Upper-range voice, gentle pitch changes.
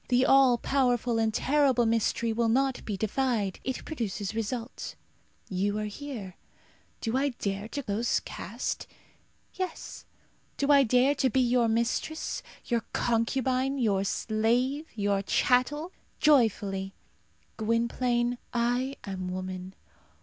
No: high, 235 Hz; average, 3.6 semitones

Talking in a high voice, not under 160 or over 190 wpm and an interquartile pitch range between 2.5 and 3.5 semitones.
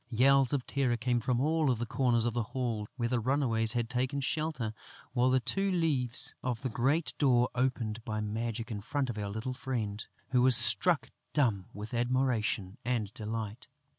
No: low, 120 Hz; average, 180 wpm; average, 2.8 semitones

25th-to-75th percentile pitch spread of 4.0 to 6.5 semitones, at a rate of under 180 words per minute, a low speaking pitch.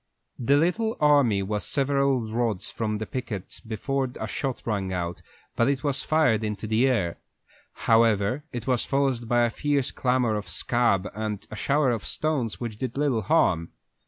Yes: average, 4.3 semitones; average, 170 wpm; low, 120 Hz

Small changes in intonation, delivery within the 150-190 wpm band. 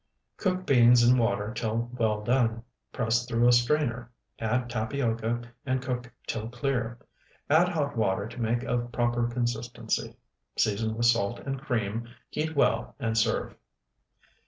No: narrow, 1.7 semitones; average, 140 wpm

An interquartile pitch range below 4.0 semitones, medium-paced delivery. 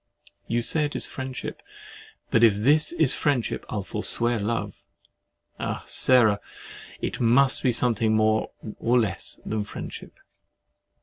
No: average, 3.0 semitones; slow, 125 wpm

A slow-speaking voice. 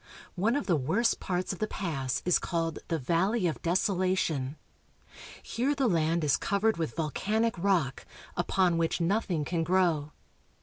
No: average, 160 wpm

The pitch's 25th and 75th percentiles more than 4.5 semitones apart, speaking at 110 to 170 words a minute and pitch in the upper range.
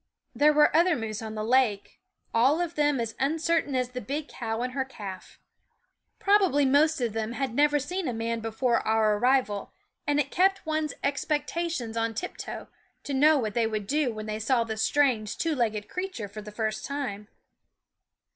No: average, 5.0 semitones; average, 185 wpm; very high, 255 Hz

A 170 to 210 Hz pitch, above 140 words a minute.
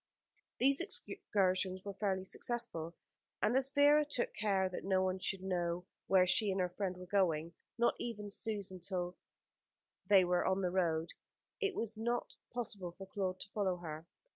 Yes: high, 190 Hz; average, 170 wpm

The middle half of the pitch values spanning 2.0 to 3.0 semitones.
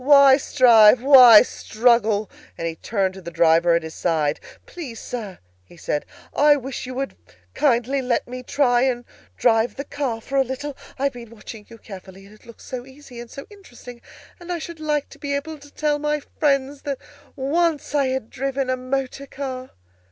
No: average, 3.8 semitones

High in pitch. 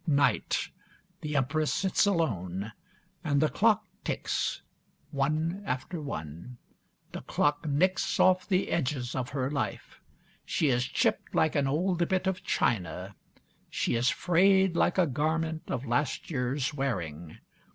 No: medium, 145 Hz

